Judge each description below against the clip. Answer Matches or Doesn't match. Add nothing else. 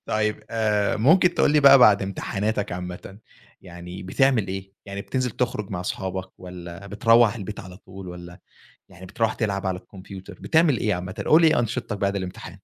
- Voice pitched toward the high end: Doesn't match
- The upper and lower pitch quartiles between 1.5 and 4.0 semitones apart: Matches